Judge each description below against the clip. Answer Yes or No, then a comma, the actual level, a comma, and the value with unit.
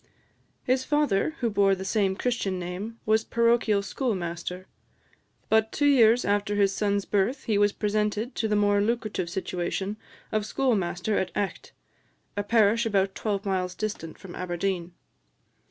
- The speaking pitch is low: No, high, 205 Hz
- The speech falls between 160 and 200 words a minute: No, average, 145 wpm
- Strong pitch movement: No, narrow, 2.6 semitones